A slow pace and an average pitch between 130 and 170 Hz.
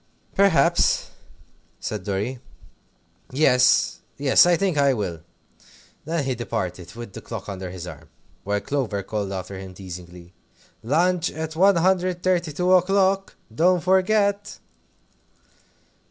Yes: slow, 110 wpm; low, 135 Hz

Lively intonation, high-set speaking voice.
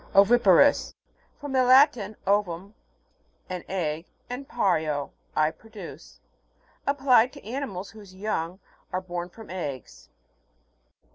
Yes: wide, 5.7 semitones; high, 200 Hz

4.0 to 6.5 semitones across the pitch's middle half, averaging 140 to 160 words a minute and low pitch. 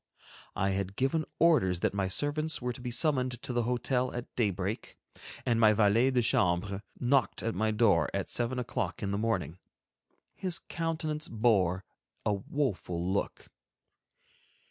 Yes: average, 4.7 semitones; average, 150 wpm; low, 115 Hz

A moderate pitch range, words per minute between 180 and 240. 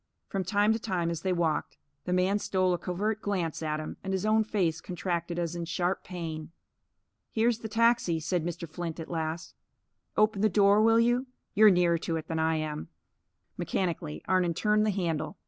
Yes: average, 3.9 semitones; average, 190 wpm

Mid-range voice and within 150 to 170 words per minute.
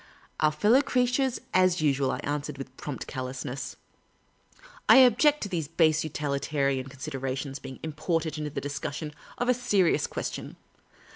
Yes: medium, 150 Hz; average, 160 wpm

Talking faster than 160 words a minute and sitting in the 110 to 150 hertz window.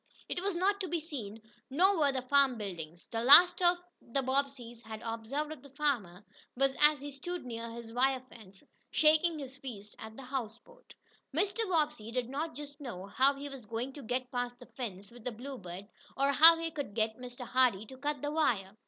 No: average, 200 wpm; very high, 265 Hz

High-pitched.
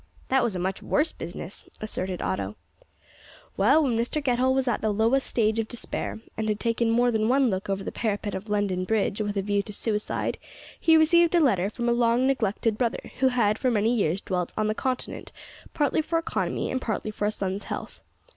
Yes: high, 220 Hz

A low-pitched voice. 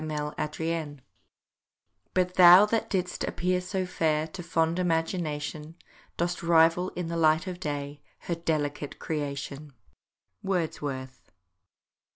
No: medium, 165 Hz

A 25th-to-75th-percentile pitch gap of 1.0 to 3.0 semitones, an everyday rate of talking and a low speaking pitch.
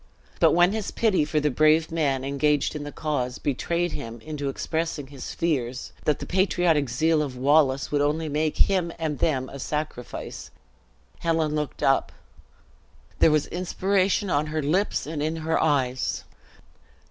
No: average, 2.7 semitones; average, 160 wpm; medium, 150 Hz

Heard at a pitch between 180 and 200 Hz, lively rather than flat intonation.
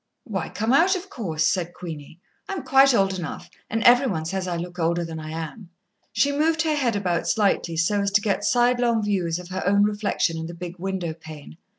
Yes: high, 190 Hz; wide, 6.0 semitones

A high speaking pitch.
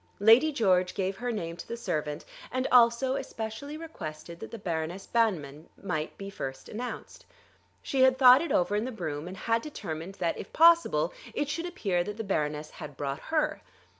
Yes: high, 205 Hz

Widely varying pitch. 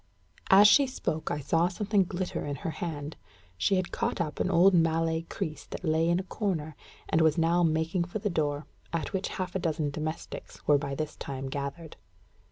No: average, 3.2 semitones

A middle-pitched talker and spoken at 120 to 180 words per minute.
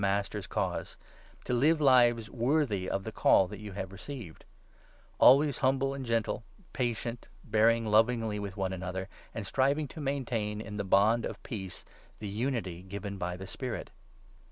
No: low, 110 Hz; average, 170 wpm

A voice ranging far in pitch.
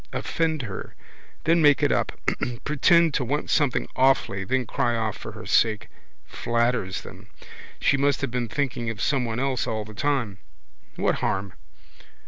No: average, 4.2 semitones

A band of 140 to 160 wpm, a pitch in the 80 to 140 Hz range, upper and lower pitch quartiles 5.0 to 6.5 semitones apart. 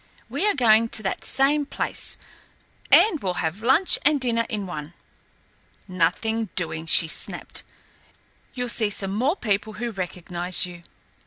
No: average, 145 wpm; high, 215 Hz; wide, 5.5 semitones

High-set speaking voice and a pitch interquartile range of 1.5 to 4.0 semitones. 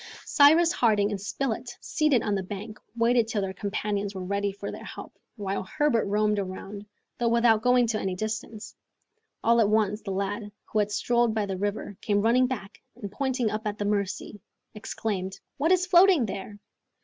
Yes: high, 215 Hz; average, 2.9 semitones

